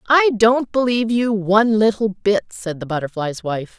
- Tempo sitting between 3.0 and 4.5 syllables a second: No, 4.9 syllables/s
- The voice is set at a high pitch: Yes, high, 205 Hz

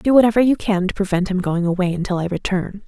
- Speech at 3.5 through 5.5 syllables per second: No, 6.4 syllables/s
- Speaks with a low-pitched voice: No, high, 195 Hz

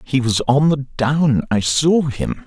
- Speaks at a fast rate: No, average, 170 wpm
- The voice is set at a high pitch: No, medium, 140 Hz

